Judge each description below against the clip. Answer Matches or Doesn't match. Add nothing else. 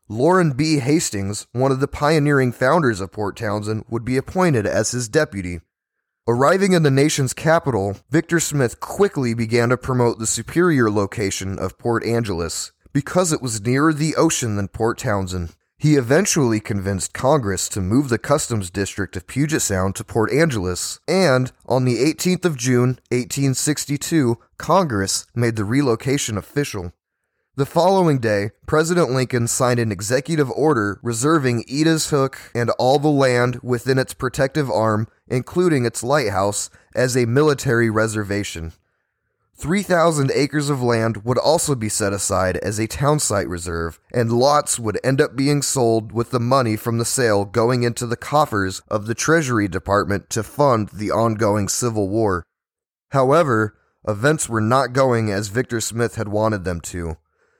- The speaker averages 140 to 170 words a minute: Matches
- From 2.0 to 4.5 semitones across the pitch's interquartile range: Doesn't match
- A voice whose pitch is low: Matches